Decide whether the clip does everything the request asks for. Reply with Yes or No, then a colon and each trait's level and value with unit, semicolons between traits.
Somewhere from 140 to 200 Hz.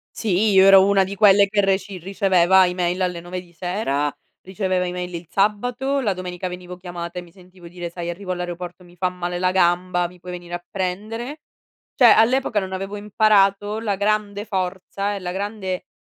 Yes: medium, 185 Hz